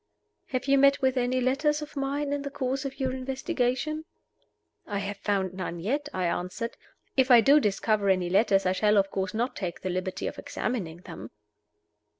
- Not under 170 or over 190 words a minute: Yes, average, 185 wpm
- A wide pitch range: Yes, wide, 6.0 semitones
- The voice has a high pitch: Yes, high, 245 Hz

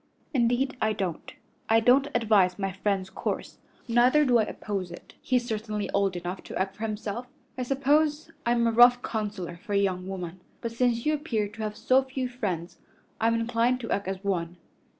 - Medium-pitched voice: No, high, 220 Hz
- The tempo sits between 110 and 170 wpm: No, average, 190 wpm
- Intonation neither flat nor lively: Yes, average, 4.1 semitones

